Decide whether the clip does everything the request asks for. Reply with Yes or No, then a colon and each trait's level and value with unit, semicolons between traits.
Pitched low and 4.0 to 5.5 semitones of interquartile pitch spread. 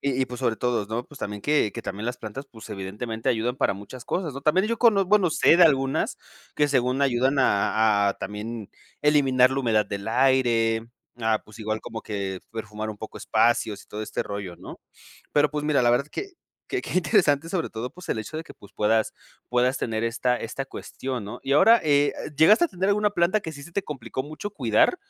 Yes: low, 125 Hz; average, 5.2 semitones